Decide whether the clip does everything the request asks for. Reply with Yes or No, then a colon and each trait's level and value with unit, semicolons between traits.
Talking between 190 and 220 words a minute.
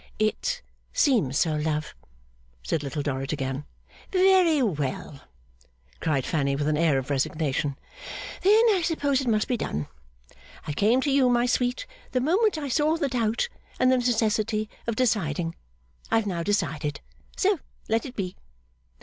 No: average, 155 wpm